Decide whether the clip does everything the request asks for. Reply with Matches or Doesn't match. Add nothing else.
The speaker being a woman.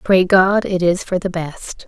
Matches